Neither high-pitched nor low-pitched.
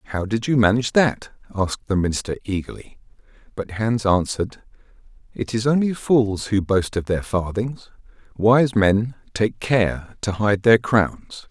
No: low, 105 Hz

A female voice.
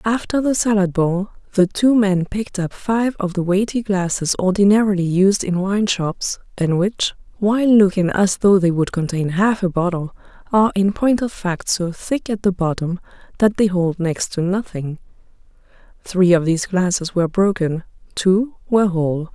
Yes: female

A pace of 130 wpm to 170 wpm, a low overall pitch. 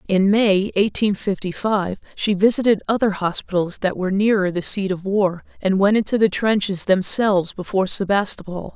No: average, 165 wpm; high, 195 Hz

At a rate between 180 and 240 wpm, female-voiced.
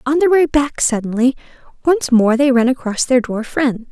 Yes: average, 200 wpm; female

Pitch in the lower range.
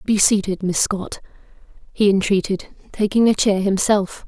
No: high, 200 Hz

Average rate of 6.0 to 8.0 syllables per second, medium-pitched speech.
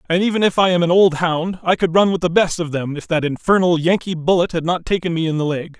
Yes: 6.1 syllables/s; medium, 170 Hz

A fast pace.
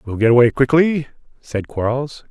No: average, 155 wpm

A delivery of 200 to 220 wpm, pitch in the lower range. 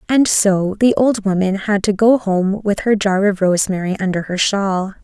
No: fast, 205 wpm; high, 200 Hz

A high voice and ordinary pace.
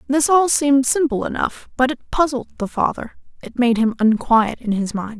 Yes: very high, 250 Hz; average, 195 wpm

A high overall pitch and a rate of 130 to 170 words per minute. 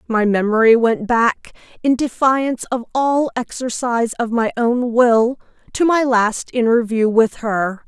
Yes: high, 235 Hz; average, 145 wpm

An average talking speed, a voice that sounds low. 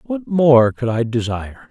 Yes: average, 175 wpm; low, 130 Hz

